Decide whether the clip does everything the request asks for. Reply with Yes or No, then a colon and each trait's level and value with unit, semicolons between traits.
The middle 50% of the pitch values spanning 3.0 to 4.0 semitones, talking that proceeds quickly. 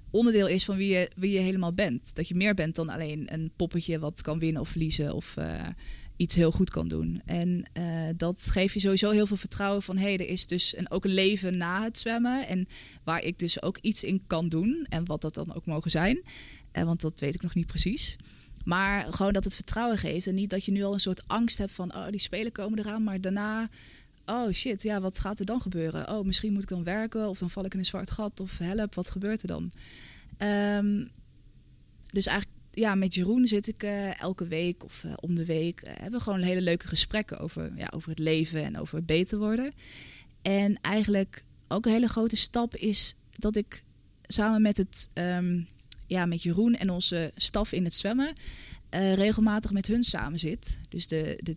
Yes: average, 3.6 semitones; fast, 225 wpm